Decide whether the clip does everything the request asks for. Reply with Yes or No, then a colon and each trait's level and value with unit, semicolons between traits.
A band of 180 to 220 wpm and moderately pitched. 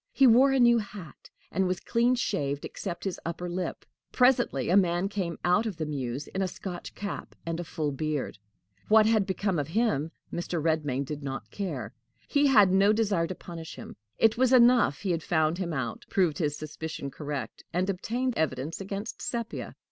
Yes: average, 190 wpm; medium, 180 Hz